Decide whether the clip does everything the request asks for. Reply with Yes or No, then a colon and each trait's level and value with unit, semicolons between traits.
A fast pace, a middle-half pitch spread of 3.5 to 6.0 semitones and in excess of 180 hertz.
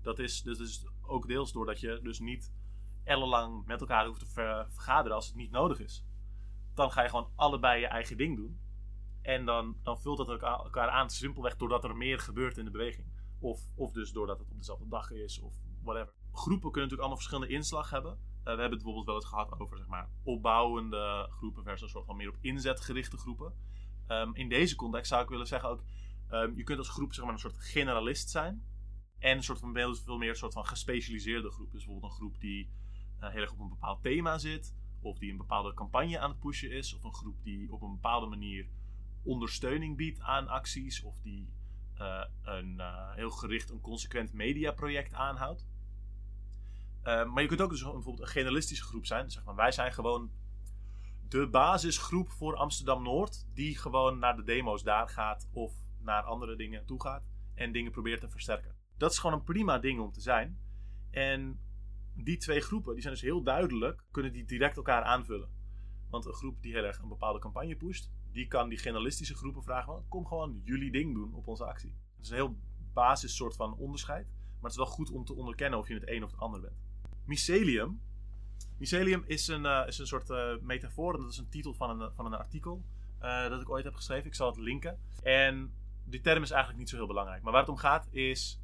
No: fast, 215 wpm; average, 4.5 semitones; low, 115 Hz